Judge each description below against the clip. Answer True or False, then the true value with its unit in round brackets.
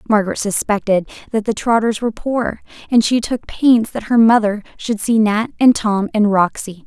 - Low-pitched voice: False (220 Hz)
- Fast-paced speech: False (185 wpm)